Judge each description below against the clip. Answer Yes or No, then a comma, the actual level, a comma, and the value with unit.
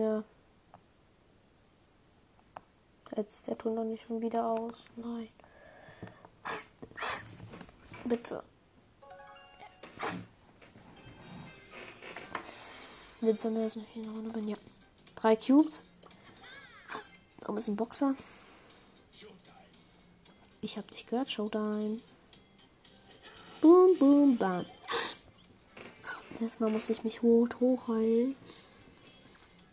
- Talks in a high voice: Yes, high, 225 Hz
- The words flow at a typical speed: No, slow, 80 wpm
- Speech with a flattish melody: Yes, narrow, 1.4 semitones